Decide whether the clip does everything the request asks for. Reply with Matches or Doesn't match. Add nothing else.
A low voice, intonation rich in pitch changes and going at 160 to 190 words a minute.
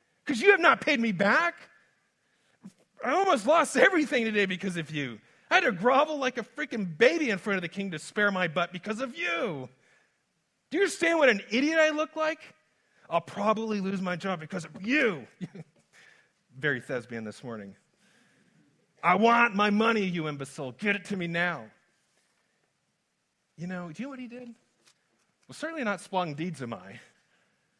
Doesn't match